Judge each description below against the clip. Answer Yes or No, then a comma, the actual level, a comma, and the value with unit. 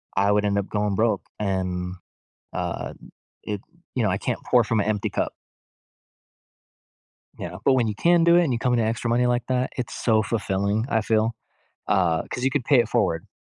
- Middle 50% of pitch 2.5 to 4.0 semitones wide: Yes, average, 3.4 semitones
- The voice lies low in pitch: Yes, low, 110 Hz